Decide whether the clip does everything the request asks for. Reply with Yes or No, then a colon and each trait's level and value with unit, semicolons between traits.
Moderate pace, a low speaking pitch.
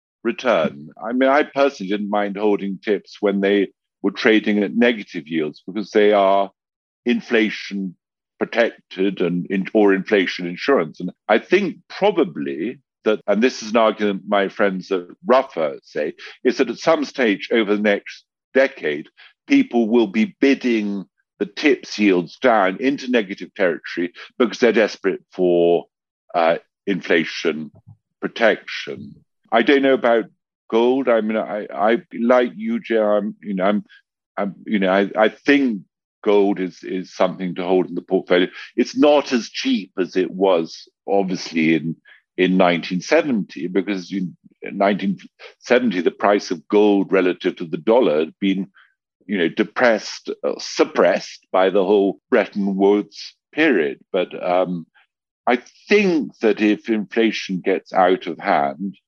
Yes: average, 145 wpm; low, 100 Hz